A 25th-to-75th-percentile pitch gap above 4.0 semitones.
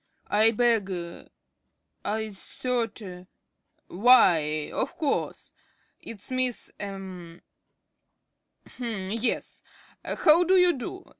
Yes: average, 5.0 semitones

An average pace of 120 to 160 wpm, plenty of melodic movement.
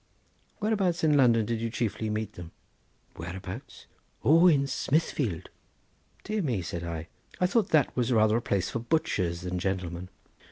Yes: average, 155 wpm; wide, 8.6 semitones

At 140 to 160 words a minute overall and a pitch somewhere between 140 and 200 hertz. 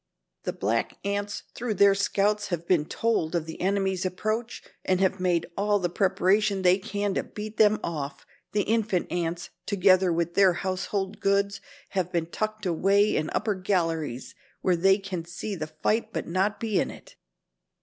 No: average, 170 wpm; high, 190 Hz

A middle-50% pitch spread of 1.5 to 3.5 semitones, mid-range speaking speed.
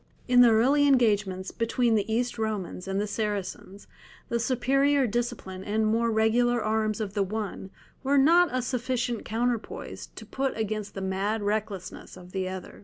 Yes: average, 3.2 semitones; average, 165 wpm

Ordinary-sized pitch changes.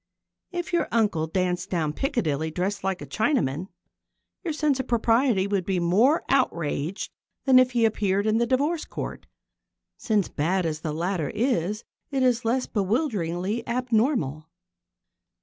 No: wide, 6.4 semitones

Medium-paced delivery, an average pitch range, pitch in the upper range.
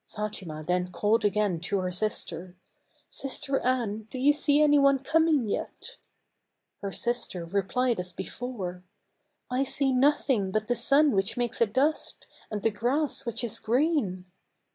No: average, 160 wpm; wide, 5.9 semitones; high, 230 Hz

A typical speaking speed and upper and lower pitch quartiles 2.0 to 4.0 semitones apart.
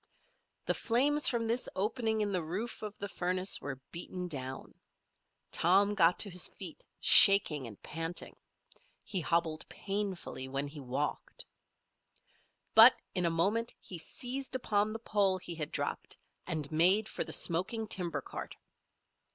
No: average, 145 wpm; average, 4.8 semitones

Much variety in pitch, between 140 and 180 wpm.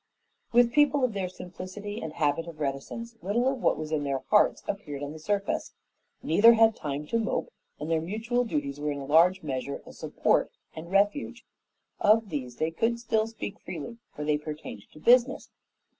No: wide, 7.0 semitones; average, 190 wpm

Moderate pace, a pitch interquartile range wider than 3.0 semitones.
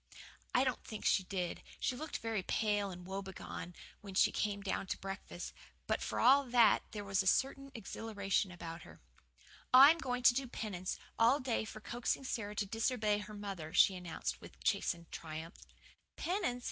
Yes: average, 170 wpm; average, 4.5 semitones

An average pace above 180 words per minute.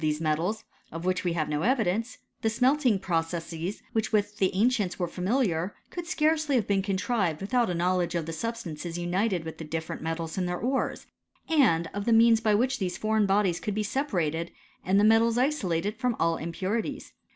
Yes: average, 195 wpm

